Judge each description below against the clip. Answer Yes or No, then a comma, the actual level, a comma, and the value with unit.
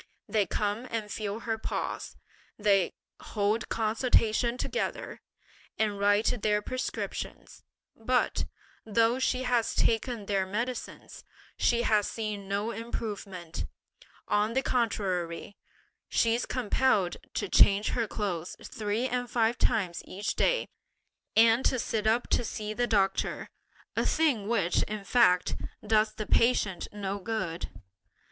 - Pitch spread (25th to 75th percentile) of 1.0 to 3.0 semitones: Yes, narrow, 2.6 semitones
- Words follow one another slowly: Yes, slow, 125 wpm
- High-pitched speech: Yes, high, 215 Hz